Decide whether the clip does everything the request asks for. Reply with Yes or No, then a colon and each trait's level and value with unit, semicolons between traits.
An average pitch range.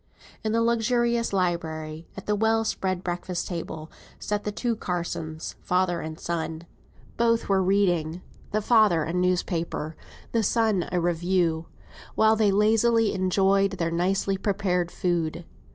Yes: average, 3.9 semitones